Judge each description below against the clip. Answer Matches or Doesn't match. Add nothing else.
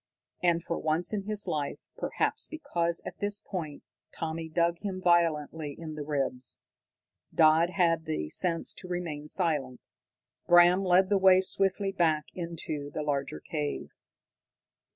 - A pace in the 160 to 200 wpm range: Doesn't match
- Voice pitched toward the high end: Doesn't match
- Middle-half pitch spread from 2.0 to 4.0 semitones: Matches